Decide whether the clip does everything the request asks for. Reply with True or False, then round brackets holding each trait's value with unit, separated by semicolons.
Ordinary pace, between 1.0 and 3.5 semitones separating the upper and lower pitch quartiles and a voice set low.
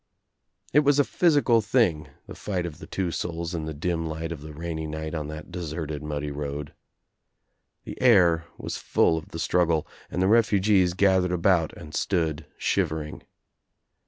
True (170 wpm; 3.2 semitones; 85 Hz)